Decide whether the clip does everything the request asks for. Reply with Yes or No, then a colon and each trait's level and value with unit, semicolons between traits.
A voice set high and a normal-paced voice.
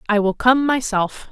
Yes: high, 230 Hz; average, 185 wpm